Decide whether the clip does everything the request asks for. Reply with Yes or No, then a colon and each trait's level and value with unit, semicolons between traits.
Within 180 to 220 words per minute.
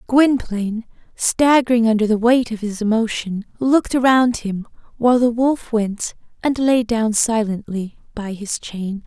No: average, 145 wpm